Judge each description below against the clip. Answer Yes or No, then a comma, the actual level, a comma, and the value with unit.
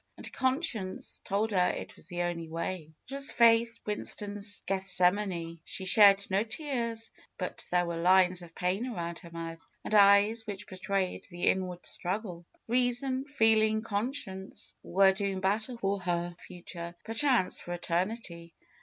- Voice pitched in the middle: No, high, 195 Hz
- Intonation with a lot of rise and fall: No, average, 4.0 semitones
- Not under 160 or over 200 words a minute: No, average, 145 wpm